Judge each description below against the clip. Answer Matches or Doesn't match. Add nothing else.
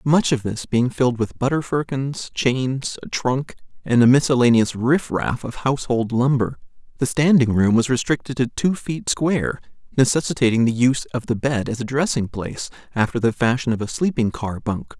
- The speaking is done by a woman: Doesn't match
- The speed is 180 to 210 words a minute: Matches